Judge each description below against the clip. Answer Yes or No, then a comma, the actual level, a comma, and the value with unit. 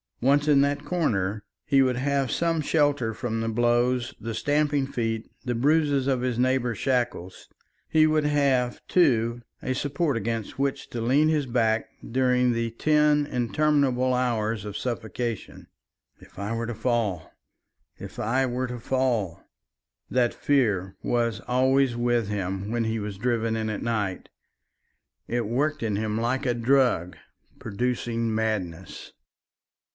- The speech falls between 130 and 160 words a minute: Yes, average, 145 wpm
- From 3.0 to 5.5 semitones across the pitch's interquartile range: Yes, average, 3.3 semitones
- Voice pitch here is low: Yes, low, 120 Hz